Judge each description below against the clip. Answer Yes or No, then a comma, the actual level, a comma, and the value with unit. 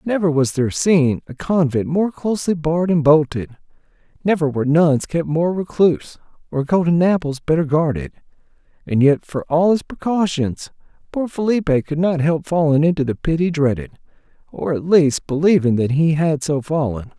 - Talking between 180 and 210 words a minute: No, average, 165 wpm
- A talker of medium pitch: Yes, medium, 155 Hz